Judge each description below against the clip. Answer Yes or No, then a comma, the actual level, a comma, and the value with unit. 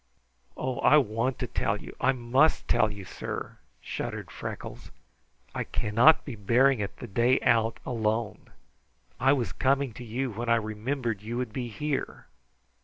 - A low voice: Yes, low, 120 Hz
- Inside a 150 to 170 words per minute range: Yes, average, 160 wpm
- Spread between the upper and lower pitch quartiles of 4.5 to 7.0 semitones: No, average, 3.2 semitones